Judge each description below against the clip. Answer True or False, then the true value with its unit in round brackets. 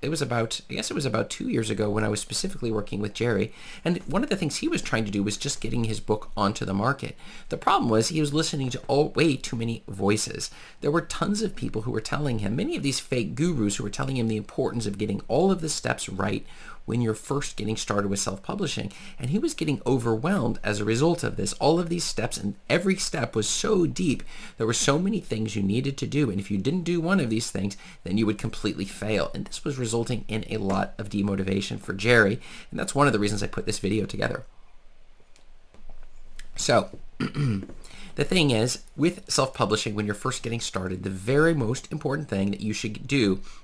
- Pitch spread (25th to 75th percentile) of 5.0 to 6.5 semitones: True (5.5 semitones)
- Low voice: True (115 Hz)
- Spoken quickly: True (230 wpm)